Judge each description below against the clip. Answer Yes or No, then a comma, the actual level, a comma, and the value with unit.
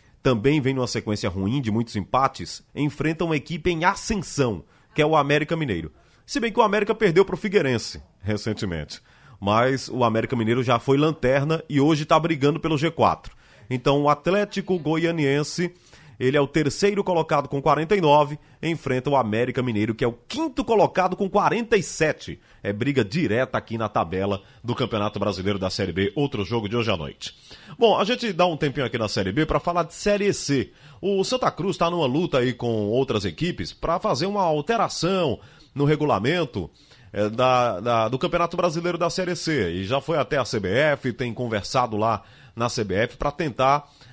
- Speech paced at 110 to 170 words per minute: No, average, 180 wpm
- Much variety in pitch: Yes, wide, 6.1 semitones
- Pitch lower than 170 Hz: Yes, medium, 140 Hz